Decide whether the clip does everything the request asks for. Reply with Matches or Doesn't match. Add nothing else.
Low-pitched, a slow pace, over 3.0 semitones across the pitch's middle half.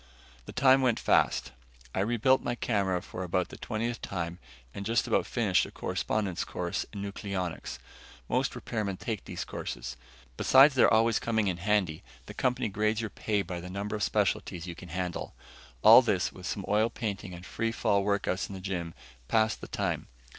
Doesn't match